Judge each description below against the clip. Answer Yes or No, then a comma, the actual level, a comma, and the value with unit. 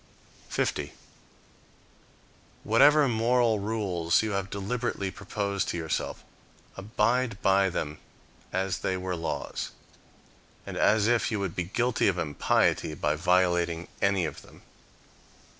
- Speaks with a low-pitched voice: Yes, low, 100 Hz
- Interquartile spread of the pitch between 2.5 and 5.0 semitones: Yes, average, 4.0 semitones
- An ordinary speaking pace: No, slow, 120 wpm